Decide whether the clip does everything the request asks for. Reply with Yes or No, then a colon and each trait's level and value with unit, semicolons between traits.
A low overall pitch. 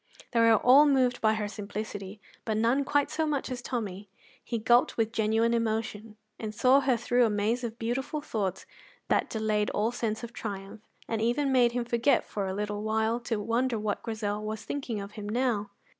No: high, 225 Hz